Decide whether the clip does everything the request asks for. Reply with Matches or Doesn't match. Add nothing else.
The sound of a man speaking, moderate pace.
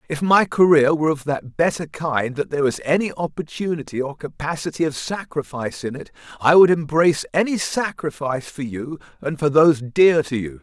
Matches